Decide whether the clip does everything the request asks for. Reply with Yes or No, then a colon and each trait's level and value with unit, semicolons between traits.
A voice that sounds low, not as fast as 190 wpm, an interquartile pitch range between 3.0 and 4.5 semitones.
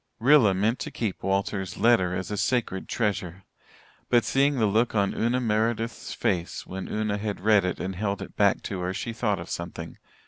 No: low, 105 Hz; average, 200 wpm; average, 3.3 semitones